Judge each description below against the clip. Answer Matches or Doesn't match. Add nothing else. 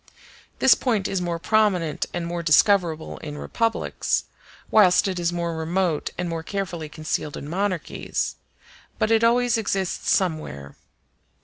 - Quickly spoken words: Doesn't match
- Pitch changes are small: Doesn't match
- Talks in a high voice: Doesn't match